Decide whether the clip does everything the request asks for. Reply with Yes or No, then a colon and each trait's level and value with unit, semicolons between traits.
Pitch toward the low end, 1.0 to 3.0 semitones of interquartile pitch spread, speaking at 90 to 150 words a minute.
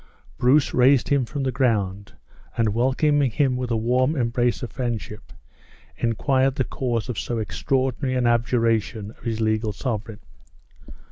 Yes: low, 120 Hz; average, 2.7 semitones; average, 145 wpm